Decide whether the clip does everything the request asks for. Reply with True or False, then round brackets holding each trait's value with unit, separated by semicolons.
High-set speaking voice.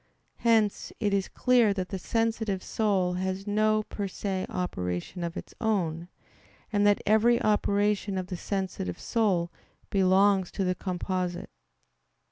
True (195 Hz)